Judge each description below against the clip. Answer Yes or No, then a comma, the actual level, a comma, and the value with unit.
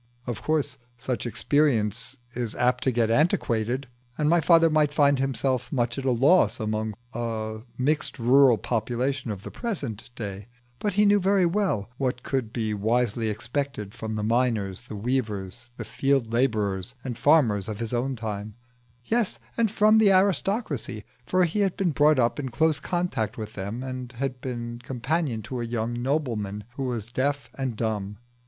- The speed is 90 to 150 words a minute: No, average, 170 wpm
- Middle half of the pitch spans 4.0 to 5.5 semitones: Yes, average, 4.5 semitones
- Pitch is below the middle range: Yes, low, 125 Hz